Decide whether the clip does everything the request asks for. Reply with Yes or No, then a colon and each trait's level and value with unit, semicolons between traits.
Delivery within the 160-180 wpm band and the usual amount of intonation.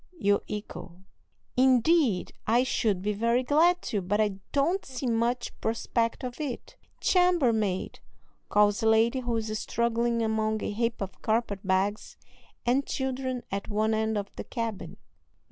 No: average, 145 wpm; average, 3.1 semitones